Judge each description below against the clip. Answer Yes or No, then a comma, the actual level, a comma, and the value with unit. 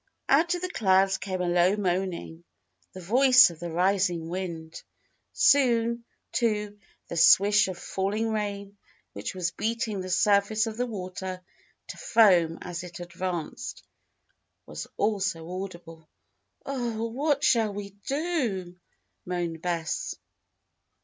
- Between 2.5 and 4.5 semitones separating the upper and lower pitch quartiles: Yes, average, 4.2 semitones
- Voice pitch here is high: Yes, high, 195 Hz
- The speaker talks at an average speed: No, slow, 125 wpm